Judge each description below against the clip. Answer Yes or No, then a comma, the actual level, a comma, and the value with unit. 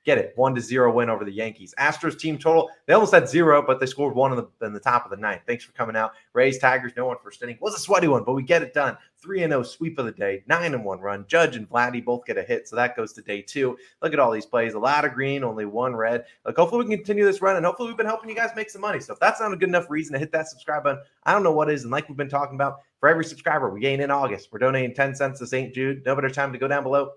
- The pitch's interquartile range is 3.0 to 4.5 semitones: No, average, 4.9 semitones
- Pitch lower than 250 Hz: Yes, medium, 140 Hz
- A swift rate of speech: Yes, fast, 320 wpm